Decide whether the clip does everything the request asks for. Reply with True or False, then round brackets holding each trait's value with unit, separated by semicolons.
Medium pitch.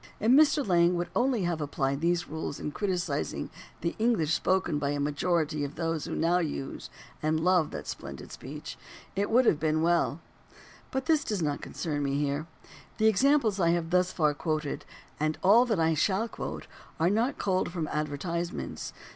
True (170 Hz)